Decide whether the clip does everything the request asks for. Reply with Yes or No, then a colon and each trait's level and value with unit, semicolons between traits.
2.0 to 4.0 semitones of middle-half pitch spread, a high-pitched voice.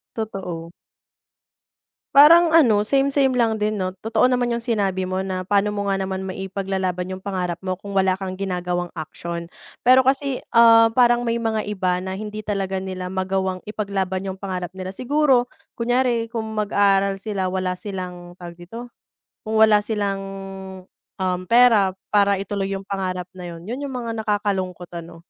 Yes: average, 3.4 semitones; high, 195 Hz